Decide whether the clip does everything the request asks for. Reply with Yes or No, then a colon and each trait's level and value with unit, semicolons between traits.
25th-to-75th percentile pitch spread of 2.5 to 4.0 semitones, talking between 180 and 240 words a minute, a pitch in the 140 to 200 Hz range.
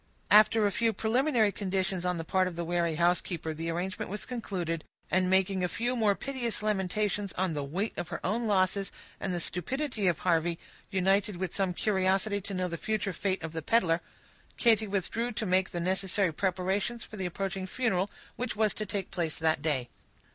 Yes: average, 3.2 semitones; average, 190 wpm; high, 190 Hz